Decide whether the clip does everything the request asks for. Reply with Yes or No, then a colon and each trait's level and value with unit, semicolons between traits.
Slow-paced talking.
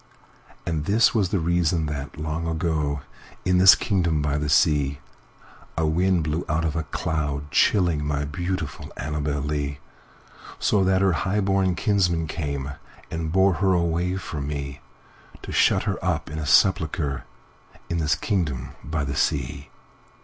Yes: slow, 130 wpm